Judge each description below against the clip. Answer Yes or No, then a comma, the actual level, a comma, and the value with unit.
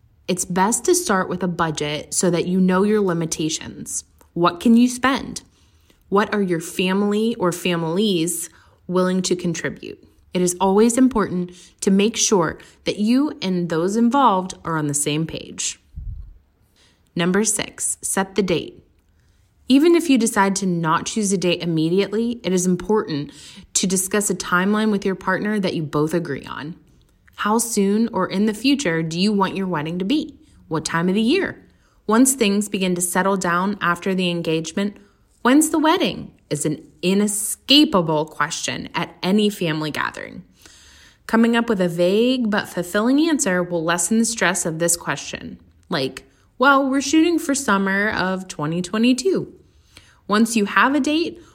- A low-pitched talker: No, medium, 185 Hz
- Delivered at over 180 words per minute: No, average, 160 wpm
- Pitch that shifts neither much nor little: Yes, average, 4.4 semitones